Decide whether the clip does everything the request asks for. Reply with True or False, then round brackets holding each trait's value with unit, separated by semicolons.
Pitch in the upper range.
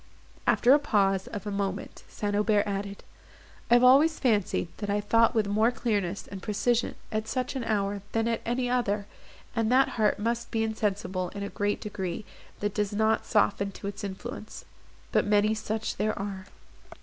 True (210 Hz)